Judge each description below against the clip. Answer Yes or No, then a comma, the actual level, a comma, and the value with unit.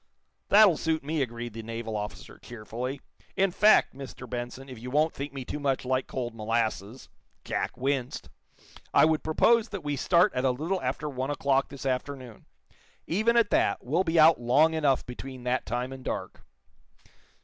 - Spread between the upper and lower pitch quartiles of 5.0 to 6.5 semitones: No, average, 4.3 semitones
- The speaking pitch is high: No, low, 135 Hz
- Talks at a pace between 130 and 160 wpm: No, average, 175 wpm